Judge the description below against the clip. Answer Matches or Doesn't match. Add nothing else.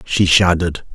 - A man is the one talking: Matches